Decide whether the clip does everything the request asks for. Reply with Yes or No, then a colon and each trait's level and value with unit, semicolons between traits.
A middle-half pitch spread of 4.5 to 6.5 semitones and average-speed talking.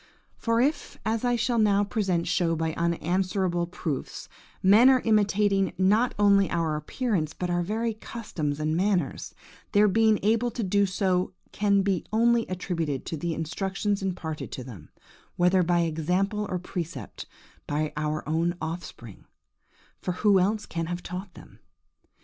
No: average, 4.0 semitones; average, 145 wpm